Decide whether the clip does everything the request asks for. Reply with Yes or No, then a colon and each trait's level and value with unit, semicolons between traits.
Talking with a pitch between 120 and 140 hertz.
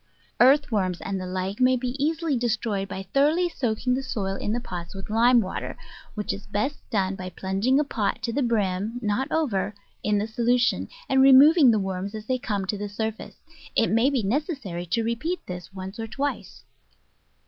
No: high, 225 Hz